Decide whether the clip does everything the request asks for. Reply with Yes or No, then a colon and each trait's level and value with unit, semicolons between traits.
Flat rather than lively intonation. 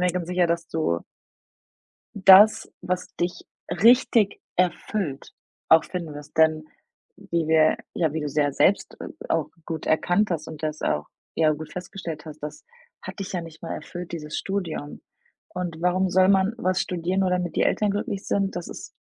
No: average, 3.2 semitones